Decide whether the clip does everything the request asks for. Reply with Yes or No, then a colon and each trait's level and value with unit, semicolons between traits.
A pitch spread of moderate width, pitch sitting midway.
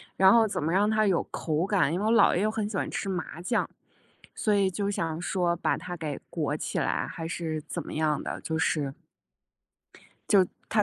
Yes: average, 4.2 semitones; medium, 180 Hz